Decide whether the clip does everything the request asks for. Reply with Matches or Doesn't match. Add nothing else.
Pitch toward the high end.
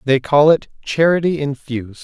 Doesn't match